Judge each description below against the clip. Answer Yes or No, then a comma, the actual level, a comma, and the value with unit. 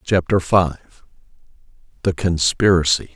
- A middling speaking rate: No, slow, 75 wpm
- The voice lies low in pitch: Yes, very low, 85 Hz